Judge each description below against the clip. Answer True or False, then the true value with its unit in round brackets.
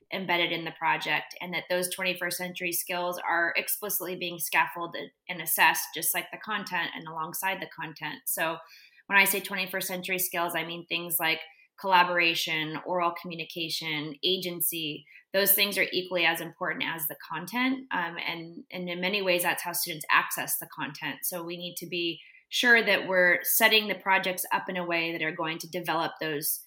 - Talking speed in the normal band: True (180 wpm)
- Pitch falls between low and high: True (175 Hz)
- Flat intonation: True (2.1 semitones)